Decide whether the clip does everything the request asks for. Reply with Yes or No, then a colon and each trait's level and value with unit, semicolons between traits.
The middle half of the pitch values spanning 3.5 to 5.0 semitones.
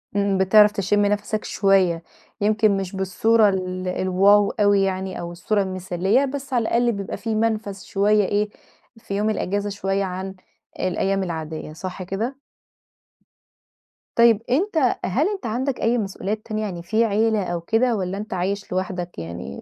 No: average, 2.8 semitones